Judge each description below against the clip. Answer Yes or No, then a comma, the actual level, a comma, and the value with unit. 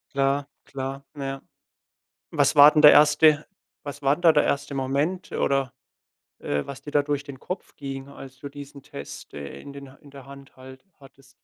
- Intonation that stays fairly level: Yes, narrow, 1.3 semitones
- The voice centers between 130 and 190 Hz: Yes, medium, 140 Hz